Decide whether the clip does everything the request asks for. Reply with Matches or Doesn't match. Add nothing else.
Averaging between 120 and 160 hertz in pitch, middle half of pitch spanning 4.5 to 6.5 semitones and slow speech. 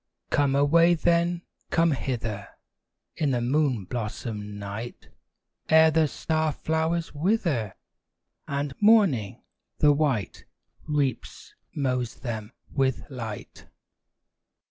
Matches